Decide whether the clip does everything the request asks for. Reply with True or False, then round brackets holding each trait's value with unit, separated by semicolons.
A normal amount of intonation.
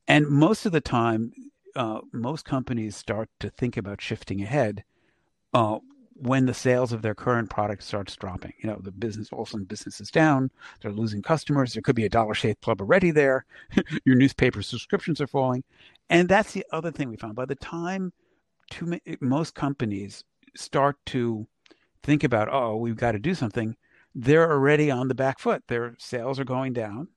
True (5.0 semitones)